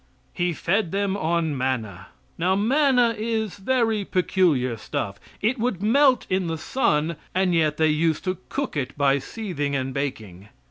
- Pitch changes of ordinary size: No, wide, 7.2 semitones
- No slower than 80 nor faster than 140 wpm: No, average, 155 wpm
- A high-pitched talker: No, medium, 175 Hz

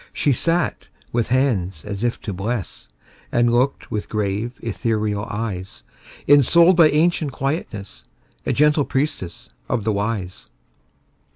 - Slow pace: Yes, slow, 125 wpm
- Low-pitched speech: Yes, low, 115 Hz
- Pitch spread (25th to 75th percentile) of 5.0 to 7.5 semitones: Yes, wide, 5.6 semitones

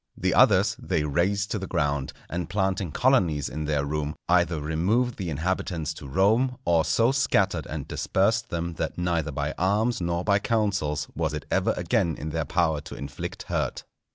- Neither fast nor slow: Yes, average, 180 wpm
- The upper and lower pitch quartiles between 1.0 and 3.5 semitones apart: No, average, 4.6 semitones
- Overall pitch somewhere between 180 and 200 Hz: No, very low, 85 Hz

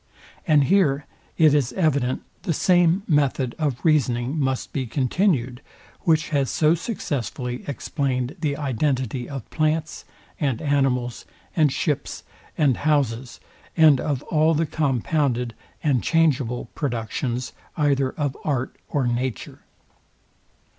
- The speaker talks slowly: Yes, slow, 120 wpm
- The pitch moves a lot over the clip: No, average, 3.5 semitones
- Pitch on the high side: No, medium, 140 Hz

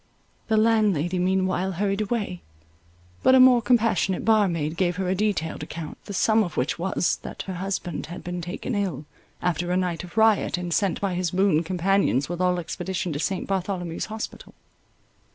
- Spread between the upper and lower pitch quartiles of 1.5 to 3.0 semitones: Yes, narrow, 2.6 semitones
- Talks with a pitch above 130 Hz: Yes, medium, 185 Hz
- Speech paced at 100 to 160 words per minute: No, average, 180 wpm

